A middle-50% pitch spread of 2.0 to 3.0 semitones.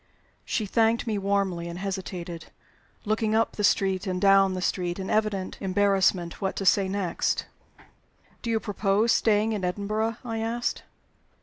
Yes: narrow, 2.5 semitones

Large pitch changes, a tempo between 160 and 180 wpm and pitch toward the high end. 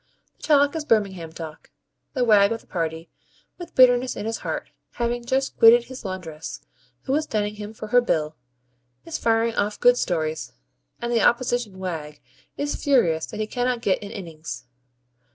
Yes: wide, 5.9 semitones; average, 170 wpm; high, 220 Hz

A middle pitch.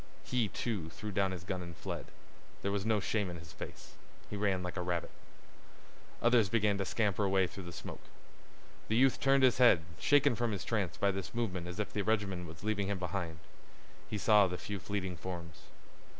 No: low, 100 Hz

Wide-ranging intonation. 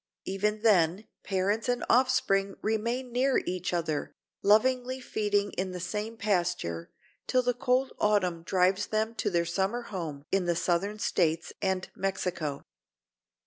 No: average, 4.1 semitones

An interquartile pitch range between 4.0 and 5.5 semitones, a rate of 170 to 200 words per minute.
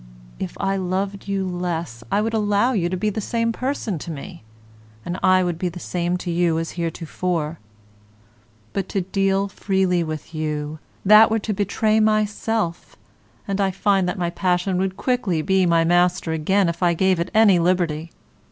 No: average, 2.8 semitones; average, 180 wpm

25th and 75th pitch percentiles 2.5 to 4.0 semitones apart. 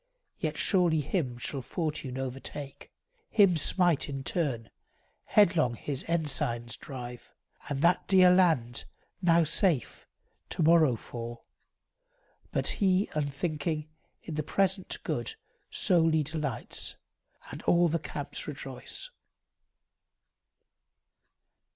No: average, 4.7 semitones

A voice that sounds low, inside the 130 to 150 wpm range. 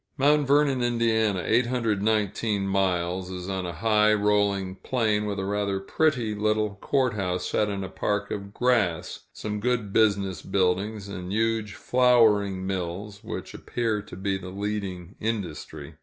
Yes: low, 105 Hz; average, 145 wpm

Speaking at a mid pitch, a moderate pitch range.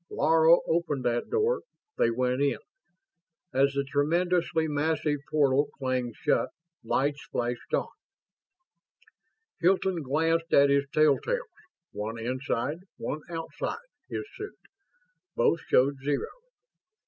Yes: medium, 145 Hz; average, 3.7 semitones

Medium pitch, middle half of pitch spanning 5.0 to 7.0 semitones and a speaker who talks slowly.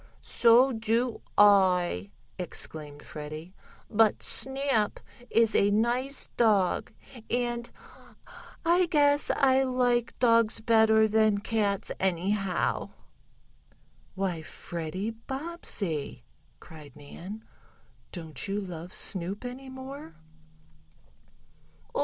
No: high, 215 Hz; average, 5.3 semitones; slow, 85 wpm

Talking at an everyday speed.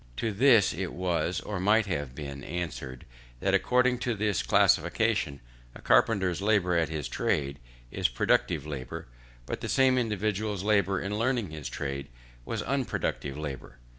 Yes: average, 150 wpm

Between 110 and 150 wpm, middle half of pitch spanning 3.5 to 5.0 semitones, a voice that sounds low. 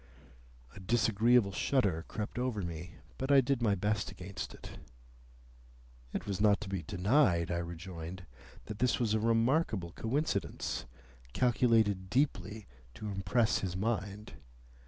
Yes: slow, 135 wpm; average, 4.2 semitones; low, 105 Hz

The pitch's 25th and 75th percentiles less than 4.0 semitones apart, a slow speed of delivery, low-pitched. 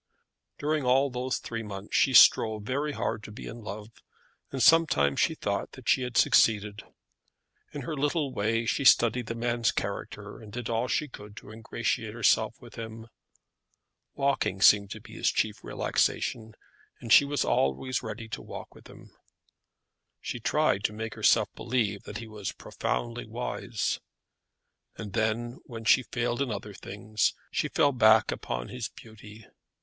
No: average, 2.9 semitones; average, 165 wpm; low, 115 Hz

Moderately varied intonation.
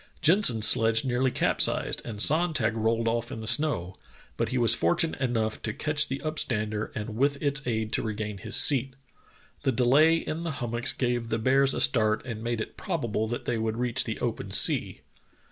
Yes: average, 3.6 semitones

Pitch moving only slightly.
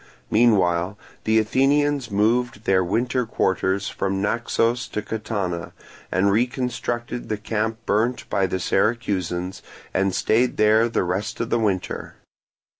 No: average, 3.6 semitones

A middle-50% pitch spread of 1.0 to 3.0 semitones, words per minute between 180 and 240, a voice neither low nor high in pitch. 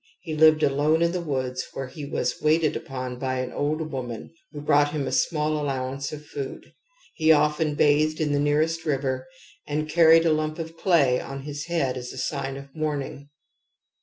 Yes: narrow, 2.5 semitones; average, 190 wpm; medium, 145 Hz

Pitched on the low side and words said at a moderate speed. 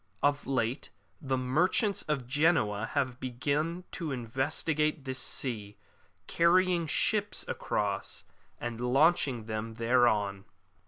No: low, 130 Hz; slow, 105 wpm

